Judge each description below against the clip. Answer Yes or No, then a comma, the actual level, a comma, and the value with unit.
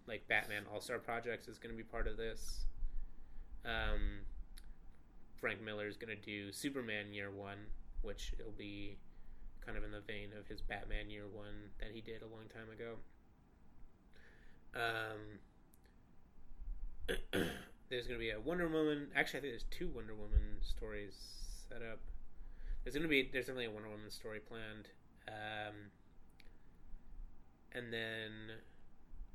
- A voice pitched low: Yes, low, 105 Hz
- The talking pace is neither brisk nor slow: Yes, average, 150 wpm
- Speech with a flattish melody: Yes, narrow, 2.2 semitones